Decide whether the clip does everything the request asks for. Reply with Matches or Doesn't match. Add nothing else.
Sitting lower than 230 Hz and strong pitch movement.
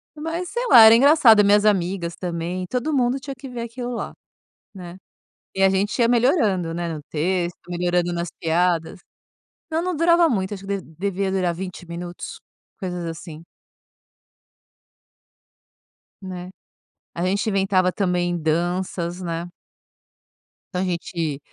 Doesn't match